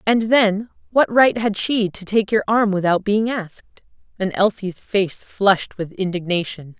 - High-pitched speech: Yes, high, 205 Hz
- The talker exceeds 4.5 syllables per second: No, 4.3 syllables/s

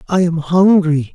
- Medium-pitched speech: Yes, medium, 170 Hz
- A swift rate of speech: No, average, 155 wpm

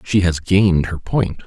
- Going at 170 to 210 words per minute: Yes, fast, 205 wpm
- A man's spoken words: Yes, male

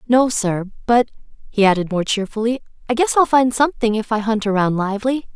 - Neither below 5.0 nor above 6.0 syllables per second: Yes, 5.9 syllables/s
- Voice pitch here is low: No, high, 225 Hz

